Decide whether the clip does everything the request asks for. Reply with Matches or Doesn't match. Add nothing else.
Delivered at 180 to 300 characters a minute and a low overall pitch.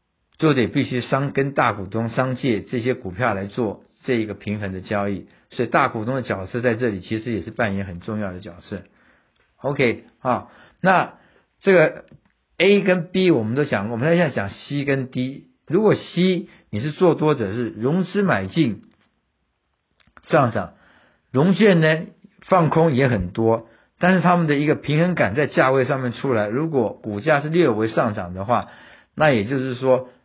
Matches